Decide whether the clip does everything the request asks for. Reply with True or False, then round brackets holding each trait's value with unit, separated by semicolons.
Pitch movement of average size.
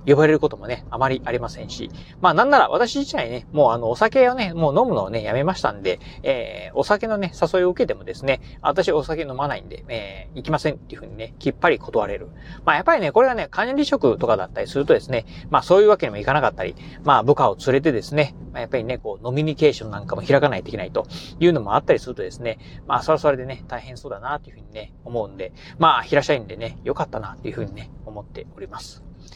False (7.2 semitones)